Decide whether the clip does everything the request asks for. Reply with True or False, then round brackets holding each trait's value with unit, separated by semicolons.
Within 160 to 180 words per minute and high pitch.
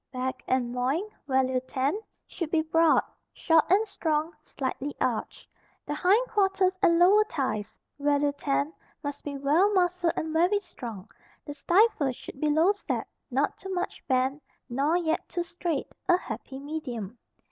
False (150 wpm; 310 Hz)